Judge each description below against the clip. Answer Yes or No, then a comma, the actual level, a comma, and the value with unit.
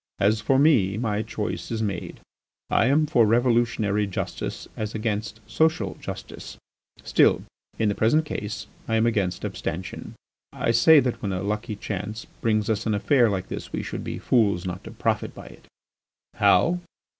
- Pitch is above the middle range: No, low, 110 Hz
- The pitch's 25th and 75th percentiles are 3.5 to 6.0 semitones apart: No, narrow, 2.5 semitones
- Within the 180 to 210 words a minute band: No, average, 170 wpm